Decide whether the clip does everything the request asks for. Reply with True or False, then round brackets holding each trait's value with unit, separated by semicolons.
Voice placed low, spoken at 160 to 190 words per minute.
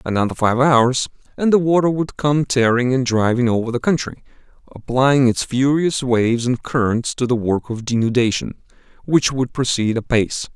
True (125 Hz; 165 wpm)